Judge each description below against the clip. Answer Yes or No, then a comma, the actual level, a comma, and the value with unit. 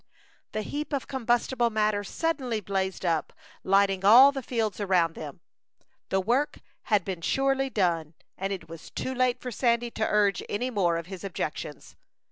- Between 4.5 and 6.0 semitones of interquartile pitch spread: Yes, average, 4.9 semitones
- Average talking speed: Yes, average, 165 wpm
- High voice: Yes, high, 210 Hz